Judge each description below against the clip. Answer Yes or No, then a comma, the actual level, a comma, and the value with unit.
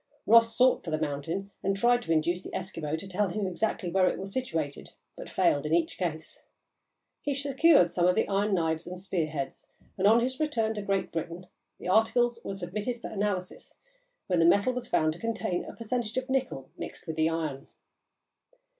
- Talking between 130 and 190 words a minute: No, average, 200 wpm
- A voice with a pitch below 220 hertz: Yes, high, 190 Hz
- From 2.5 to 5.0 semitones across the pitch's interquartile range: No, wide, 5.6 semitones